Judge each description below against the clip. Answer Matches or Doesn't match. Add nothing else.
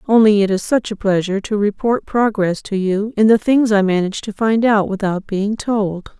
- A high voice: Matches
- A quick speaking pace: Matches